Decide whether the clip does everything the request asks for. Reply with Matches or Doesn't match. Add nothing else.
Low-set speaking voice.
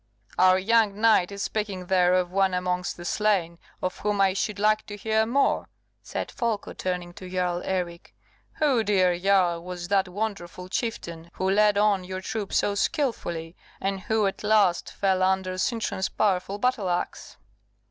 Doesn't match